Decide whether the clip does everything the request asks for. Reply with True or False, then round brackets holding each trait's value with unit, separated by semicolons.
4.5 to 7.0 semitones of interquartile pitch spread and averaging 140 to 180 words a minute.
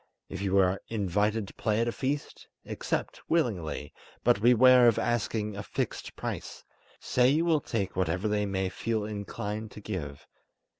False (3.3 semitones; 160 wpm)